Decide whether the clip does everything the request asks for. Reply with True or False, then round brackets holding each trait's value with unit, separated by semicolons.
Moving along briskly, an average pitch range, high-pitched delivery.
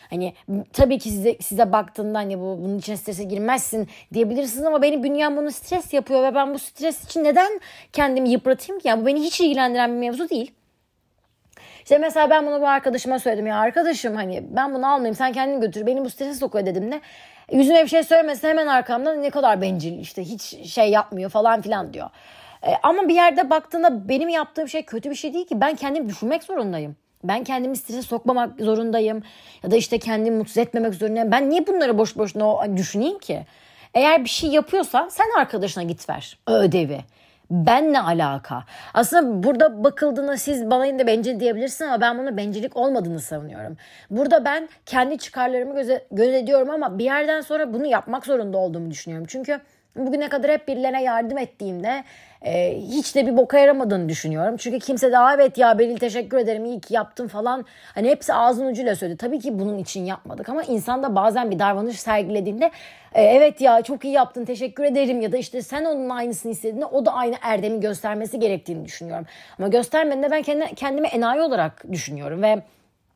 True (185 wpm; 5.0 semitones; 250 Hz)